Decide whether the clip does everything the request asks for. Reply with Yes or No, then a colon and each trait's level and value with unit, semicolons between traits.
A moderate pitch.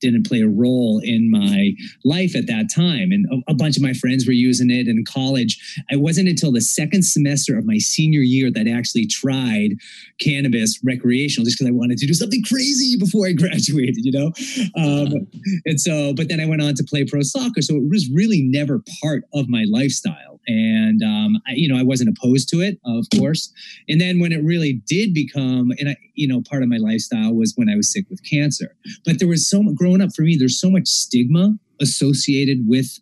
Yes: medium, 155 Hz